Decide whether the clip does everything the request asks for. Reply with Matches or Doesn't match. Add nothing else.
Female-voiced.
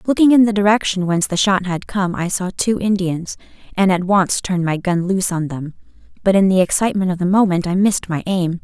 Matches